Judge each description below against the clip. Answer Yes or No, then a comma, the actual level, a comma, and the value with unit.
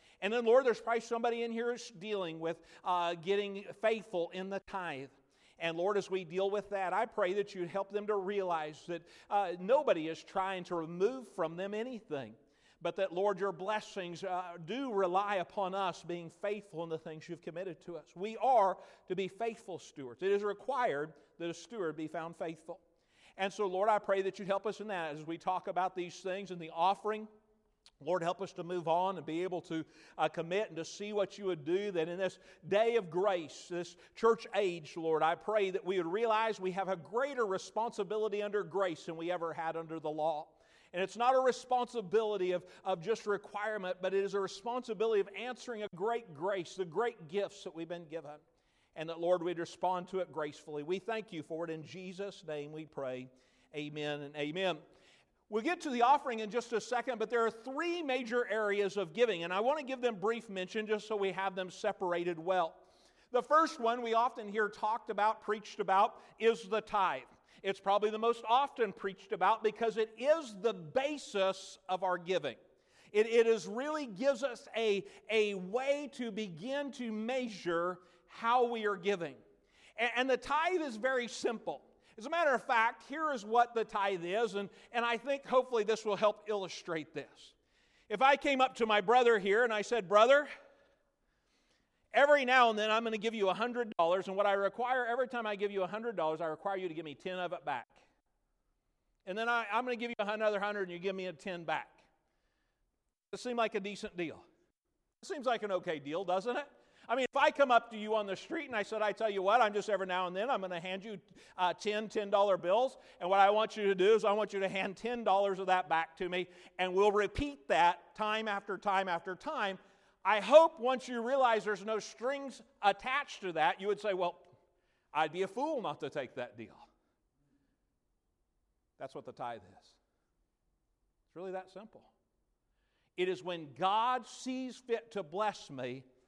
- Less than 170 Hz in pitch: No, high, 200 Hz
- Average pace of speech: No, fast, 210 wpm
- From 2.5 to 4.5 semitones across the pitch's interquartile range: Yes, average, 4.1 semitones